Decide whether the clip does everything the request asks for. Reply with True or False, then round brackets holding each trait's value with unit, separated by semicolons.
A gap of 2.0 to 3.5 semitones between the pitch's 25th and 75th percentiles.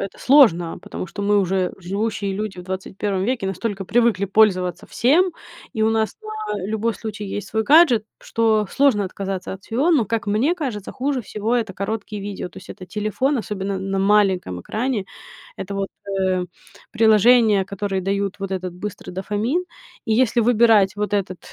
True (2.9 semitones)